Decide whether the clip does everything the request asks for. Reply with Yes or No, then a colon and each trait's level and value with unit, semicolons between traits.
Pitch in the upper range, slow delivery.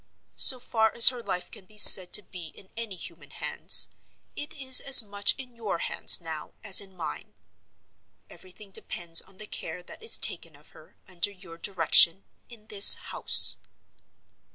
No: high, 200 Hz; average, 170 wpm